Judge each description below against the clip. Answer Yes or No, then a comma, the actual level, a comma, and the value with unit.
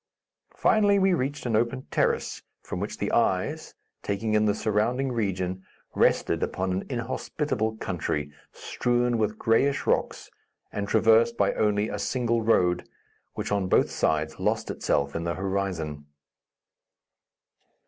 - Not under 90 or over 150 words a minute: Yes, slow, 135 wpm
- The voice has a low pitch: Yes, low, 105 Hz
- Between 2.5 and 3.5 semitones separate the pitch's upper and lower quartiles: No, average, 4.2 semitones